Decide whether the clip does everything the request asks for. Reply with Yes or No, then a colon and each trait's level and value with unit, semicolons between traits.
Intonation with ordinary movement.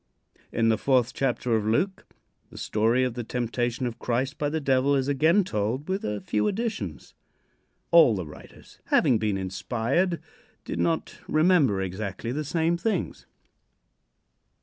No: wide, 6.2 semitones